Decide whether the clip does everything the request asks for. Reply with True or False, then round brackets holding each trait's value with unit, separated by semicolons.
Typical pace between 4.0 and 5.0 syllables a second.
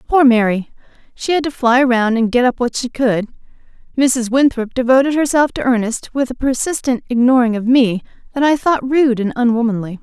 False (5.3 syllables/s)